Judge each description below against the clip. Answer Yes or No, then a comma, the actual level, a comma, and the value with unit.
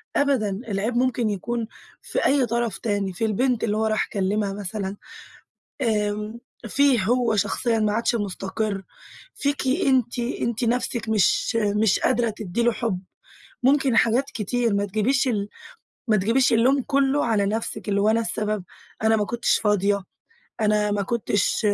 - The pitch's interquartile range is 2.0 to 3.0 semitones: Yes, narrow, 2.6 semitones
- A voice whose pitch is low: No, high, 220 Hz